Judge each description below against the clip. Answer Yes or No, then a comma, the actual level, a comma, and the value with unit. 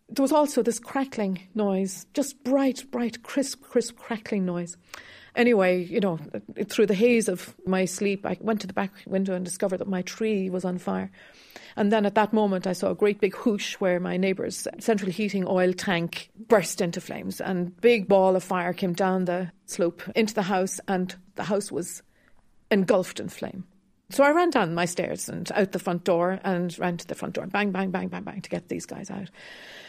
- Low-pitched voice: No, high, 195 Hz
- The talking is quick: Yes, fast, 210 wpm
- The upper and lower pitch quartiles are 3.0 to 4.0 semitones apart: Yes, average, 3.3 semitones